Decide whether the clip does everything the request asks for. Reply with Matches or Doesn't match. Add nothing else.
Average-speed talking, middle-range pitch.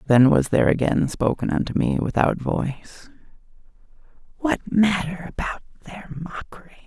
Doesn't match